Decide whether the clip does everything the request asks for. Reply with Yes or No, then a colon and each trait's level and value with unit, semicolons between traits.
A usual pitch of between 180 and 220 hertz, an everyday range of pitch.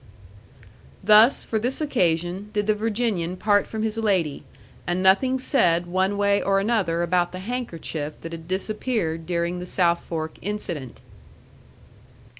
Yes: high, 190 Hz; average, 4.0 semitones